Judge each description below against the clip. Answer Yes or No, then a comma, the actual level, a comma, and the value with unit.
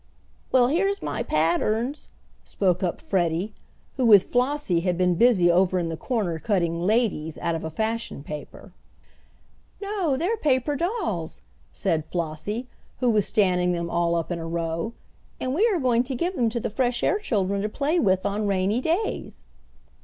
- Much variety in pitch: Yes, wide, 7.0 semitones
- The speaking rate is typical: Yes, average, 170 wpm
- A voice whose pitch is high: Yes, high, 205 Hz